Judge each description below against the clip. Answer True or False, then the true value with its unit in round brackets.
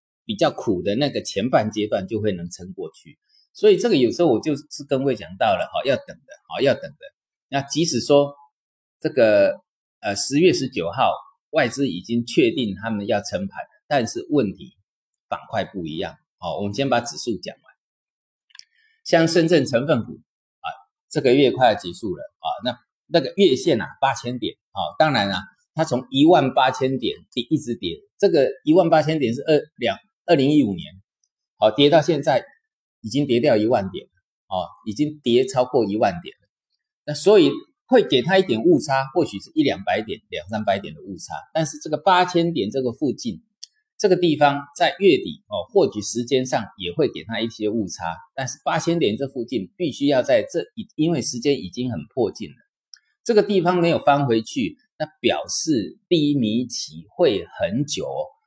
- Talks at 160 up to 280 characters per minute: True (260 characters per minute)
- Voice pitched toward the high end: False (145 Hz)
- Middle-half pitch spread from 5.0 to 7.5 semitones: False (7.9 semitones)